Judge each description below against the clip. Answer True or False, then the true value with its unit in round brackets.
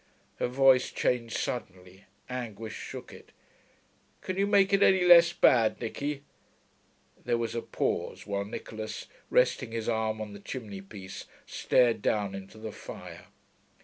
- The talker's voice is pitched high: False (115 Hz)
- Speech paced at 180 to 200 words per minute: False (145 wpm)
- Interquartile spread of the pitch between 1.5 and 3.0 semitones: False (4.3 semitones)